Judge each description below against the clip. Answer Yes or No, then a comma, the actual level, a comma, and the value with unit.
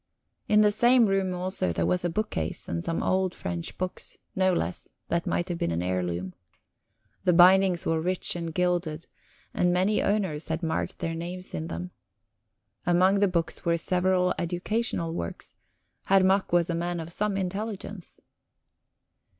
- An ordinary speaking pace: Yes, average, 160 wpm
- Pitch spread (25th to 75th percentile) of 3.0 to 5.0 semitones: No, narrow, 2.4 semitones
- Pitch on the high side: No, medium, 180 Hz